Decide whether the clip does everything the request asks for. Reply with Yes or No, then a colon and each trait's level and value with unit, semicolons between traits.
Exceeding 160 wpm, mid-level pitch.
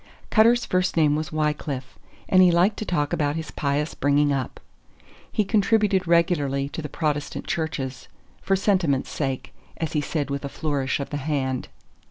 Yes: average, 170 wpm; medium, 150 Hz